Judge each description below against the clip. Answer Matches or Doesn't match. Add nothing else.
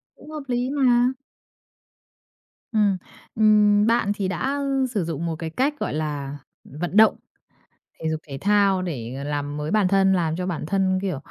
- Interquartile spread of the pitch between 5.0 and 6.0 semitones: Matches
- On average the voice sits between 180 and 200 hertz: Matches